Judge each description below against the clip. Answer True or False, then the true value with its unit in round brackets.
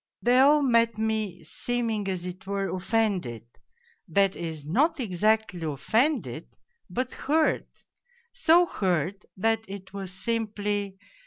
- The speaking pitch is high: True (205 Hz)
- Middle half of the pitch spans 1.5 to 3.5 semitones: False (3.9 semitones)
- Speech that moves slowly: True (115 wpm)